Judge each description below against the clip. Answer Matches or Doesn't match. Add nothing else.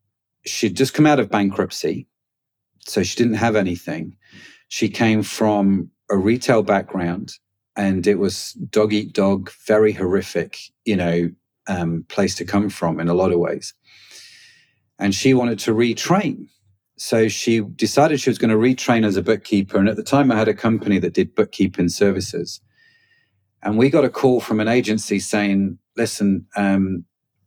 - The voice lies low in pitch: Matches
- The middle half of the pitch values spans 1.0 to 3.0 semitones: Matches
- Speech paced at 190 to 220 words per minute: Doesn't match